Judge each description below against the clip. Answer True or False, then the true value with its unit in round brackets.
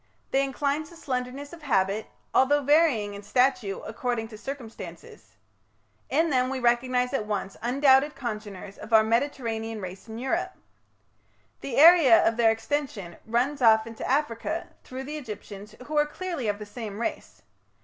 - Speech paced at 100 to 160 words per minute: True (155 wpm)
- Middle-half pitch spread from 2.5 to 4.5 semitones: True (4.2 semitones)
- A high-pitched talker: True (245 Hz)